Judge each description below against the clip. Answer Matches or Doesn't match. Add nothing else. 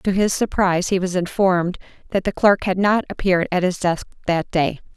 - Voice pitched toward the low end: Doesn't match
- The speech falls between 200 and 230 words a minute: Matches